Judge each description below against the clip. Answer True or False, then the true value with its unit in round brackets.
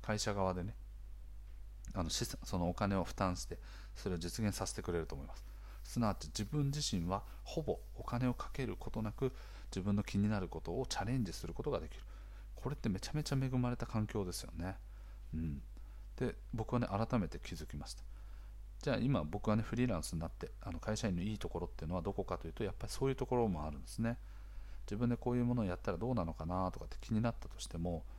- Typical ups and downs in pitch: True (3.9 semitones)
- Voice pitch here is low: True (100 Hz)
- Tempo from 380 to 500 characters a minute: True (435 characters per minute)